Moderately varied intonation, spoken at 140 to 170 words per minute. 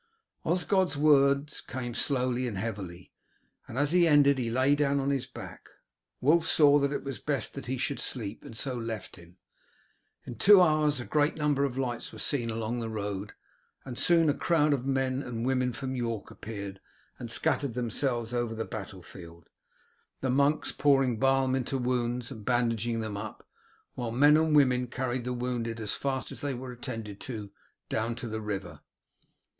No: average, 3.6 semitones; average, 180 wpm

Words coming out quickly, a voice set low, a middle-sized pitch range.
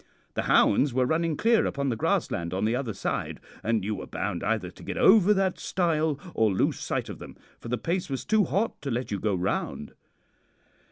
No: fast, 210 wpm; low, 130 Hz; wide, 8.1 semitones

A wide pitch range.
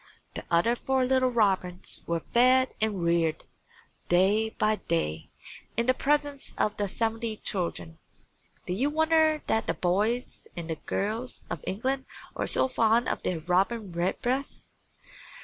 Yes: wide, 6.2 semitones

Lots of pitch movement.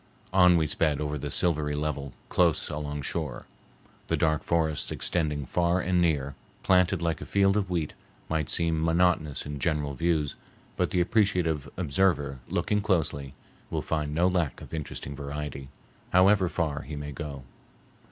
No: average, 3.3 semitones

